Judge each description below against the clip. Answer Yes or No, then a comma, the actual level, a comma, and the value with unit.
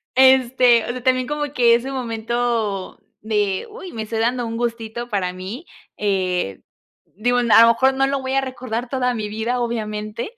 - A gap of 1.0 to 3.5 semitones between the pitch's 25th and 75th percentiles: Yes, average, 2.9 semitones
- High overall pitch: Yes, high, 235 Hz